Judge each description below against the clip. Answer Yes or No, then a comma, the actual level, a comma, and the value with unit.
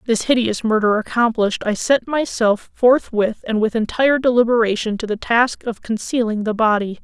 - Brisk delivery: No, average, 160 wpm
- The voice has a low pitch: No, high, 230 Hz